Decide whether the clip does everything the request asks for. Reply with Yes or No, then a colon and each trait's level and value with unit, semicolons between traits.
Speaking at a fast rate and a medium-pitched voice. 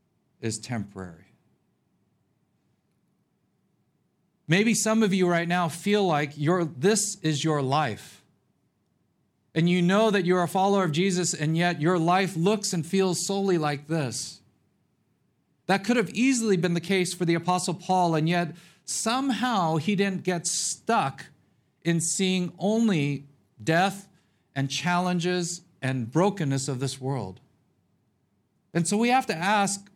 No: average, 140 wpm; medium, 175 Hz